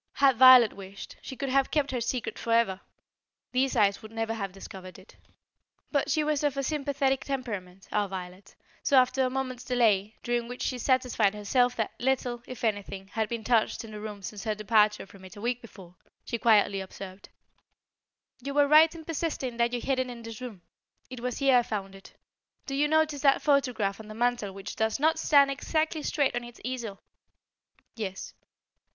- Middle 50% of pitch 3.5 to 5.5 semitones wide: Yes, average, 4.3 semitones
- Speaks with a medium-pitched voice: No, high, 240 Hz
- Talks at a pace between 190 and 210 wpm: Yes, average, 195 wpm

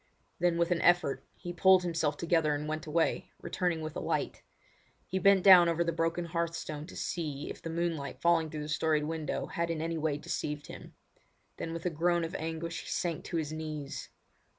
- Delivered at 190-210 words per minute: Yes, fast, 205 wpm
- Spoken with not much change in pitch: Yes, narrow, 1.8 semitones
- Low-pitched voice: No, medium, 165 Hz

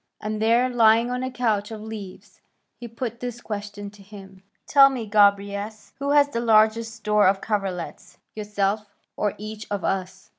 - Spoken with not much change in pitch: Yes, narrow, 2.3 semitones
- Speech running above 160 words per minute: Yes, average, 170 wpm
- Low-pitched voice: No, high, 215 Hz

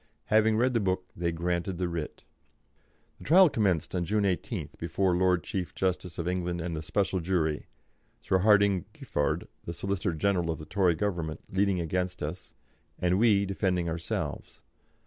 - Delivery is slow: No, average, 165 wpm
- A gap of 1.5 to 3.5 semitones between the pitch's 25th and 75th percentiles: Yes, narrow, 2.6 semitones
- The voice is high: No, very low, 90 Hz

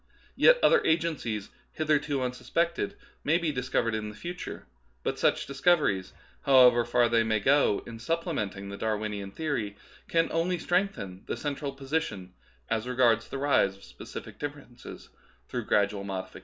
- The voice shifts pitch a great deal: Yes, wide, 6.6 semitones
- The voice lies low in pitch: Yes, low, 125 Hz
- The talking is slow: No, average, 155 wpm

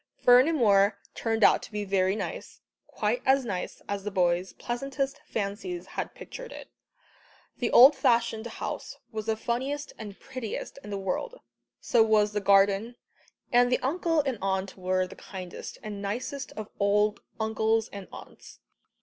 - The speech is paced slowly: No, average, 155 wpm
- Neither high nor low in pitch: No, high, 220 Hz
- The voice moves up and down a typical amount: Yes, average, 4.1 semitones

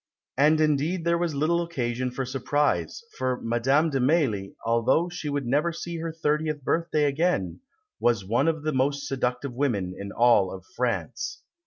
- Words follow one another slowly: No, average, 160 wpm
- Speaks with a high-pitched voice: No, medium, 140 Hz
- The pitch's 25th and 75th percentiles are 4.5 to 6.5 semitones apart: Yes, average, 4.8 semitones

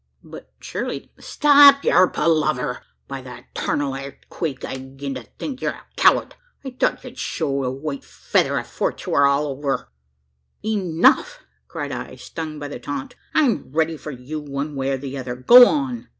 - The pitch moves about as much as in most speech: Yes, average, 4.2 semitones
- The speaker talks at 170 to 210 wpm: Yes, average, 180 wpm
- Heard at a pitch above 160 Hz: No, medium, 145 Hz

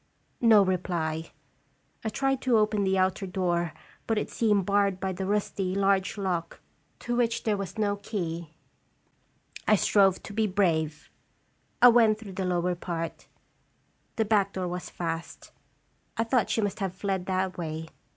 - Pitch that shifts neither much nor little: Yes, average, 3.0 semitones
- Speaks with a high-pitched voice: Yes, high, 195 Hz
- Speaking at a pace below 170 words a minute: Yes, average, 160 wpm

